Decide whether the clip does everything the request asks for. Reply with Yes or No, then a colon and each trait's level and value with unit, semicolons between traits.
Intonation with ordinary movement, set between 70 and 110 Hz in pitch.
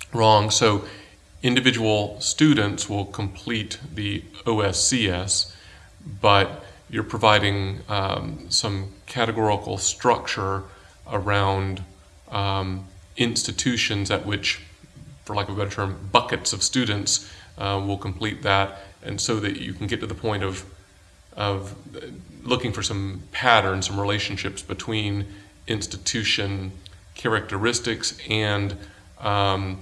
No: narrow, 2.0 semitones; low, 100 Hz